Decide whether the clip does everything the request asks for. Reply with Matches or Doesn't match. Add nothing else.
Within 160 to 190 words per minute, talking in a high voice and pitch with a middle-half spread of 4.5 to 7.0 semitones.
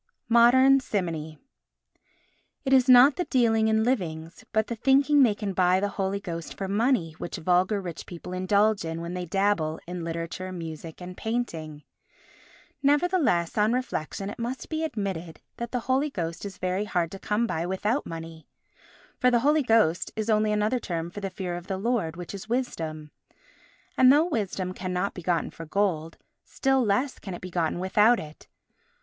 Matches